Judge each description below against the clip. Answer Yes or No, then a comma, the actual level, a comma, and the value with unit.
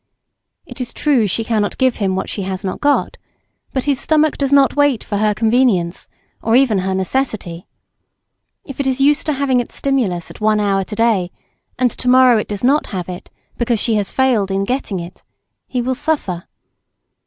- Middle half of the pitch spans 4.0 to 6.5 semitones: Yes, average, 5.2 semitones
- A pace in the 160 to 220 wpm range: Yes, average, 195 wpm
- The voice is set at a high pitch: Yes, high, 230 Hz